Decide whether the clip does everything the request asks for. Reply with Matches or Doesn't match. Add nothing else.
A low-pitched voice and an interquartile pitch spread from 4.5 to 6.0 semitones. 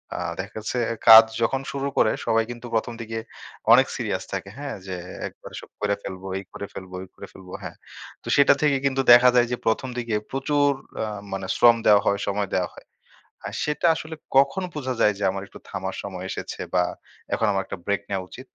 Matches